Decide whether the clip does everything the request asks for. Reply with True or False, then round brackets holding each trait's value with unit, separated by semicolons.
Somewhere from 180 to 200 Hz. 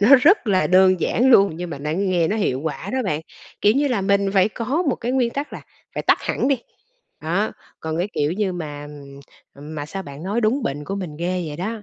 True (190 Hz)